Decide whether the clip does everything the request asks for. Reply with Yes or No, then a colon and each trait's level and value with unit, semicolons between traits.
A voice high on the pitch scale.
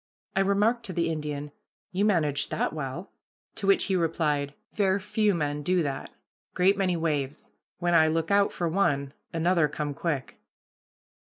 No: medium, 165 Hz